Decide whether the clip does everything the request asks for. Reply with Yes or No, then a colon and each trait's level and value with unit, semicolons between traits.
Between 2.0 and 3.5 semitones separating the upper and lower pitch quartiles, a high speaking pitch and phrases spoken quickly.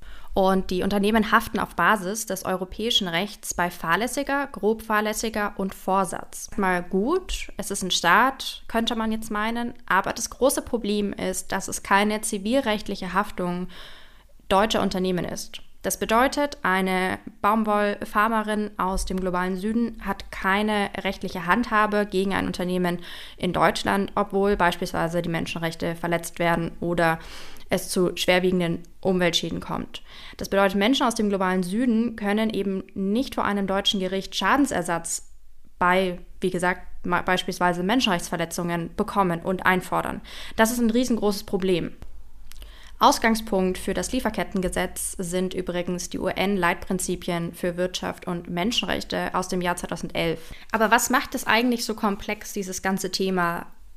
No: average, 3.0 semitones; high, 195 Hz; average, 135 wpm